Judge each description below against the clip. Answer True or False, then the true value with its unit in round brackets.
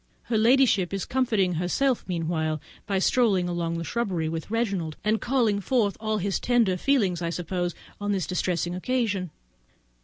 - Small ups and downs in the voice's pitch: False (4.7 semitones)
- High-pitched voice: True (195 Hz)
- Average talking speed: True (150 wpm)